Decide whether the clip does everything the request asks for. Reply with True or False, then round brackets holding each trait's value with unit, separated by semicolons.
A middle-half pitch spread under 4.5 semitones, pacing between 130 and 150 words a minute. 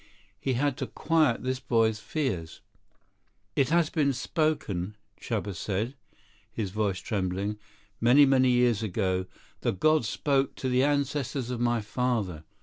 False (5.0 semitones; 140 wpm)